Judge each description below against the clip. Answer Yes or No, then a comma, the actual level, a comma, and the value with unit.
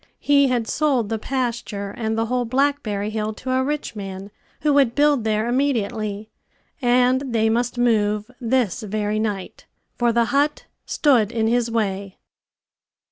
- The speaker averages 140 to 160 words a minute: Yes, average, 150 wpm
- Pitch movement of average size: Yes, average, 3.3 semitones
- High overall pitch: Yes, high, 230 Hz